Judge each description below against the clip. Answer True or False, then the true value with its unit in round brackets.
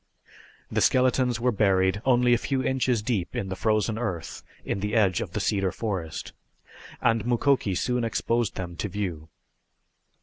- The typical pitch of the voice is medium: False (110 Hz)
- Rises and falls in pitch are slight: False (4.4 semitones)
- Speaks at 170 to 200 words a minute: False (160 wpm)